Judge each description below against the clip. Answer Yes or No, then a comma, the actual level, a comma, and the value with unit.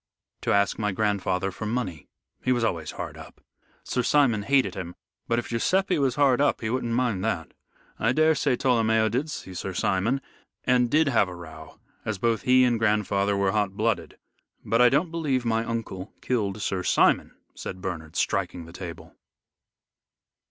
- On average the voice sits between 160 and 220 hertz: No, low, 110 Hz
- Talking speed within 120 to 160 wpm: No, average, 175 wpm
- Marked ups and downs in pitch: No, average, 4.7 semitones